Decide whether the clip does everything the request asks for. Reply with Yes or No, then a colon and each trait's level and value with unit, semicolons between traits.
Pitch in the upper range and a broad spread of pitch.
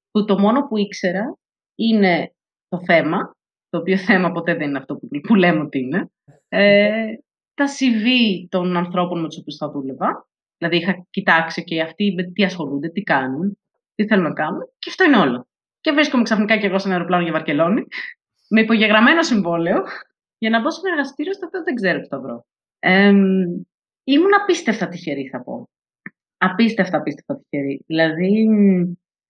No: high, 195 Hz; average, 5.0 semitones